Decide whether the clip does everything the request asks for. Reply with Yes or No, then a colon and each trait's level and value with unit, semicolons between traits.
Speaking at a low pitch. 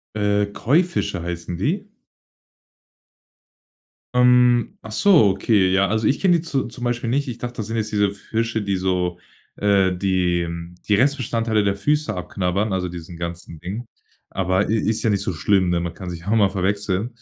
Yes: low, 105 Hz